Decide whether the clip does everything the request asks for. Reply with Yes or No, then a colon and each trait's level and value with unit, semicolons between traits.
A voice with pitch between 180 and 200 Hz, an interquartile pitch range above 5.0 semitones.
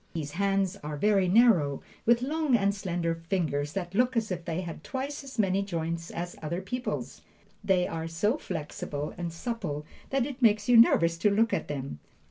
Yes: high, 190 Hz; wide, 5.5 semitones